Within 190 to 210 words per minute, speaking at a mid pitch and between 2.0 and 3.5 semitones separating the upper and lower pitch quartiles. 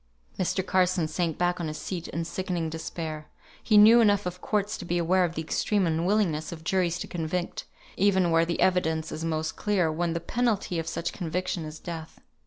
Yes: average, 195 wpm; medium, 175 Hz; narrow, 2.5 semitones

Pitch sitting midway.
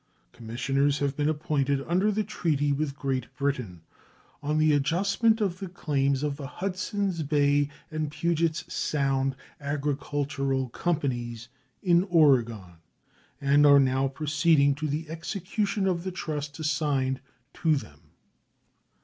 Yes: medium, 145 Hz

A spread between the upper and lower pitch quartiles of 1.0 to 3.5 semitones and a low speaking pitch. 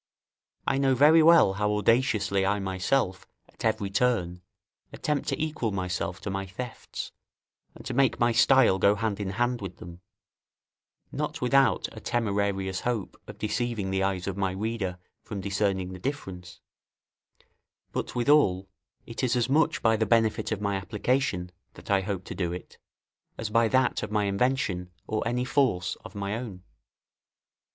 No: average, 4.2 semitones; low, 105 Hz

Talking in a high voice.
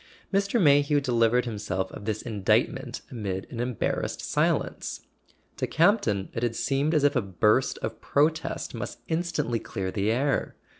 No: low, 125 Hz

